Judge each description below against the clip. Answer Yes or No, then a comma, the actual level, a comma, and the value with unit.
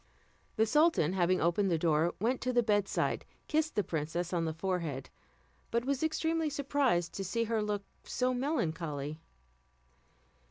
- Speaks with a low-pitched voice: No, high, 205 Hz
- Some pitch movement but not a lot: No, wide, 7.2 semitones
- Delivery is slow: No, average, 150 wpm